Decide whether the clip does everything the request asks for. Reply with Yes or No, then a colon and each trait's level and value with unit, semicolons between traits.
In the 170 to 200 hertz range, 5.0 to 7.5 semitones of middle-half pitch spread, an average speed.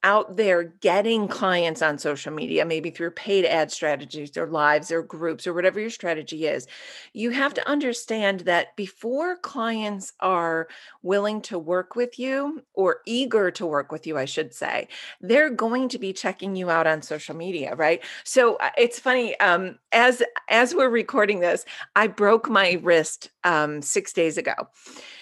Yes: high, 190 Hz; wide, 5.5 semitones; average, 170 wpm